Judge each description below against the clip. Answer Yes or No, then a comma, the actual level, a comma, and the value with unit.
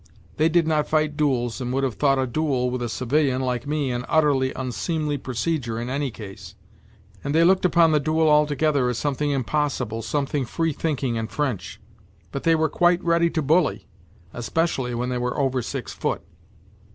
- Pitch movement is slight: No, average, 3.8 semitones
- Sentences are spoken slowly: No, average, 190 wpm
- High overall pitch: No, medium, 140 Hz